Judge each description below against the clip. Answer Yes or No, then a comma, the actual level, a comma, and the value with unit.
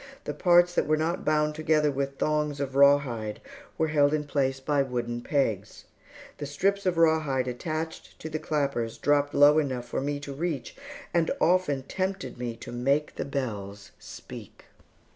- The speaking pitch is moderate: Yes, medium, 145 Hz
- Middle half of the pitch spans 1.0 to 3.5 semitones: Yes, average, 2.9 semitones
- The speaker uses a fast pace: No, average, 165 wpm